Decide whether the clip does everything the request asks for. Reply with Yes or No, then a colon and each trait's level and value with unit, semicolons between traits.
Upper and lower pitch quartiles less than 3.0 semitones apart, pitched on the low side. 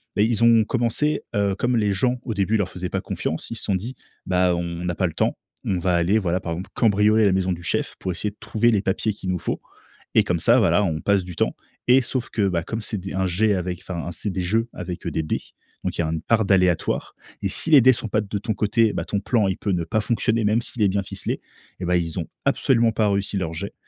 No: average, 3.6 semitones; low, 100 Hz